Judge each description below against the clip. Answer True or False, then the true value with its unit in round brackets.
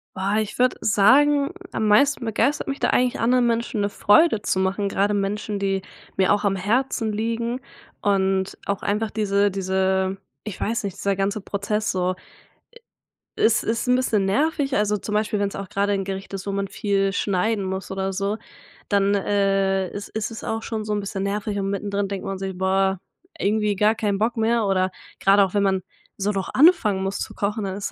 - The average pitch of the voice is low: False (200 Hz)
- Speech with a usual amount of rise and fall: False (2.1 semitones)